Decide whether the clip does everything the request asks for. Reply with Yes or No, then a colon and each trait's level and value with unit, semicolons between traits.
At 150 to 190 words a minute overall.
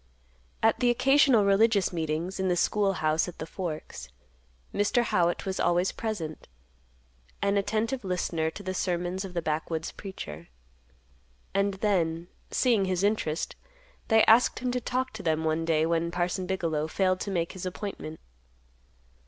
Yes: average, 155 wpm